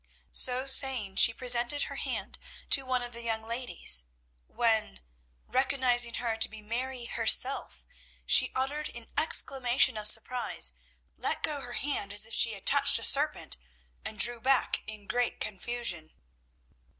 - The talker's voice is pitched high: Yes, high, 240 Hz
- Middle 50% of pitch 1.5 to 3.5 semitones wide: Yes, average, 2.8 semitones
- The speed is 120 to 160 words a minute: Yes, average, 150 wpm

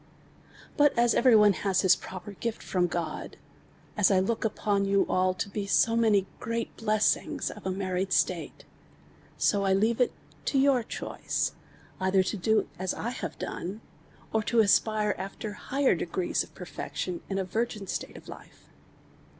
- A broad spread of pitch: No, average, 3.0 semitones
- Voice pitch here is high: Yes, high, 205 Hz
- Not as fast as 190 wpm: Yes, average, 165 wpm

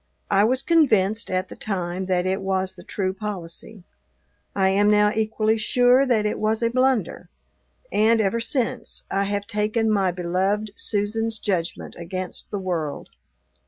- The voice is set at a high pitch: Yes, high, 205 Hz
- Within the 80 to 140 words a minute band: No, average, 155 wpm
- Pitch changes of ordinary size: Yes, average, 3.0 semitones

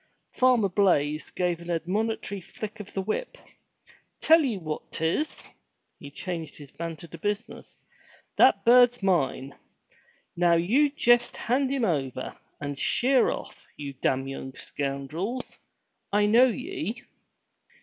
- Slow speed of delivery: Yes, slow, 130 wpm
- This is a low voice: No, high, 190 Hz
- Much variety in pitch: Yes, wide, 7.7 semitones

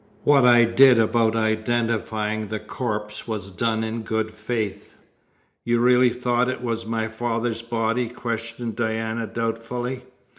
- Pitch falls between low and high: No, low, 115 Hz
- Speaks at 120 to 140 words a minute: Yes, slow, 135 wpm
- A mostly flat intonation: Yes, narrow, 1.5 semitones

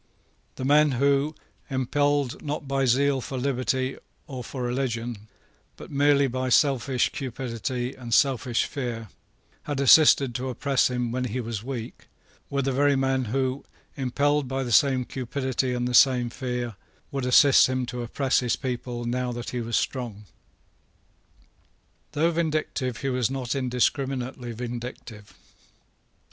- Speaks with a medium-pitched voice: No, low, 130 Hz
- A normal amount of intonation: No, narrow, 2.1 semitones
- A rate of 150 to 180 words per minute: No, average, 140 wpm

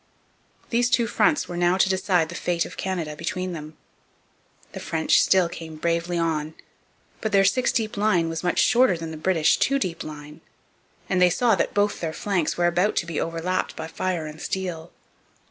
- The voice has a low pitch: No, medium, 175 Hz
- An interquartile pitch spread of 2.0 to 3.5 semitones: Yes, average, 2.8 semitones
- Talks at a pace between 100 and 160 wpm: No, average, 195 wpm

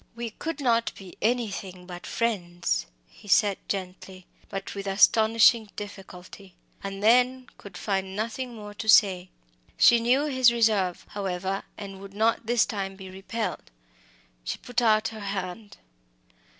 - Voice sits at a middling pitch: No, high, 205 Hz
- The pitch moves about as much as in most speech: Yes, average, 3.1 semitones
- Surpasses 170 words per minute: No, average, 140 wpm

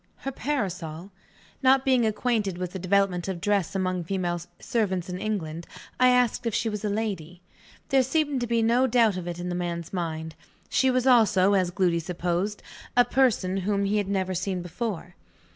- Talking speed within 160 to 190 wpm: Yes, average, 185 wpm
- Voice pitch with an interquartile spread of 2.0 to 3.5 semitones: No, average, 4.7 semitones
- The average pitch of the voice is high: Yes, high, 195 Hz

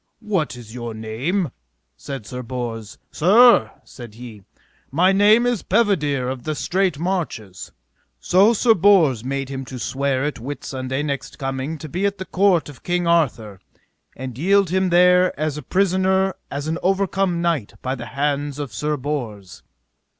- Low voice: No, medium, 150 Hz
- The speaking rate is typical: Yes, average, 160 wpm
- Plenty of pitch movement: Yes, wide, 6.5 semitones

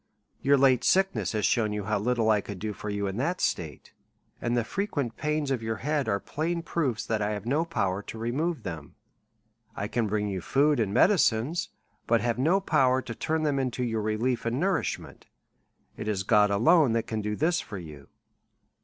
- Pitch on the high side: No, low, 115 Hz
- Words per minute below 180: No, average, 200 wpm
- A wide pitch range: Yes, wide, 5.7 semitones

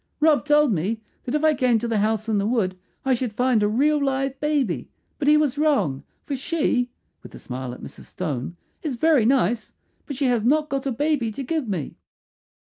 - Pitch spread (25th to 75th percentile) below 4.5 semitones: No, wide, 5.4 semitones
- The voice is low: No, very high, 250 Hz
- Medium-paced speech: No, fast, 215 wpm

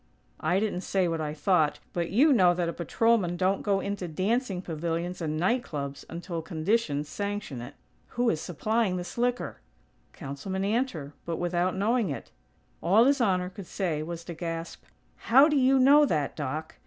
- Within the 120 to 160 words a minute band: No, average, 175 wpm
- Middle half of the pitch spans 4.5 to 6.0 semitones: Yes, average, 4.9 semitones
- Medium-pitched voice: Yes, medium, 180 Hz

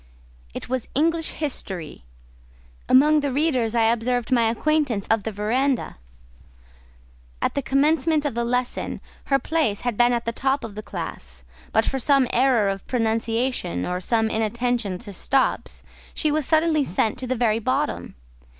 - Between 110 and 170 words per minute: Yes, average, 160 wpm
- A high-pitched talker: Yes, high, 245 Hz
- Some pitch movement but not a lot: Yes, average, 3.8 semitones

